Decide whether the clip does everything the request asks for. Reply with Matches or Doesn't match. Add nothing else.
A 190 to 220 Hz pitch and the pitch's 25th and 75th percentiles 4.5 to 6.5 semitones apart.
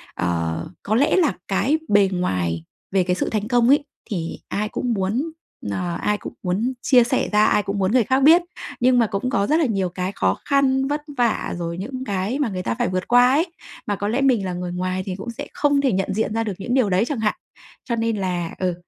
Matches